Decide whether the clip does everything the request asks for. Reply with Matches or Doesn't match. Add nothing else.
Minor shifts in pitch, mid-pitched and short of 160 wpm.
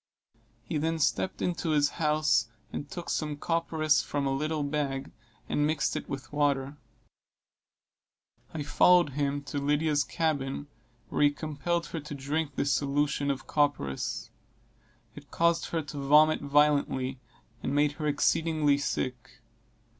Matches